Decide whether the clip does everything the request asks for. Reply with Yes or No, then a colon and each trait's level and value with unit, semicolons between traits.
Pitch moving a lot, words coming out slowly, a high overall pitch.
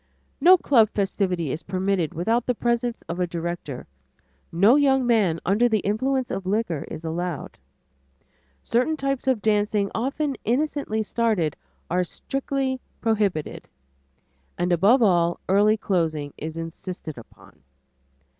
Yes: wide, 5.8 semitones; slow, 125 wpm; high, 205 Hz